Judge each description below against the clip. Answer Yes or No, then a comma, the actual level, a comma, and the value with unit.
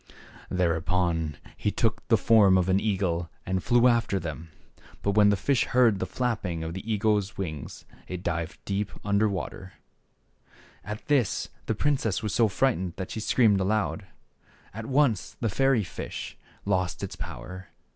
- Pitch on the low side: Yes, low, 100 Hz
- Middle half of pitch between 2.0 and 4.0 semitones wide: Yes, average, 3.4 semitones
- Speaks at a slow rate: No, average, 160 wpm